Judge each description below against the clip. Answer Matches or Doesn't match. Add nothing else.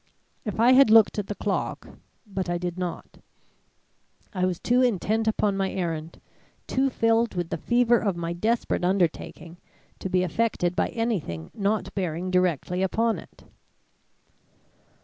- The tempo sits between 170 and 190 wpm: Doesn't match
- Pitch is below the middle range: Doesn't match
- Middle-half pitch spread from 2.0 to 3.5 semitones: Doesn't match